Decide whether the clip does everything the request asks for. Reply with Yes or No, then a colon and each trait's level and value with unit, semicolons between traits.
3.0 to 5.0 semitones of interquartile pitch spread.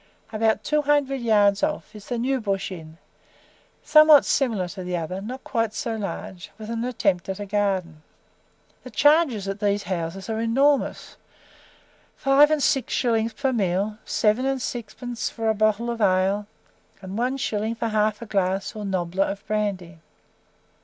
Yes: average, 3.9 semitones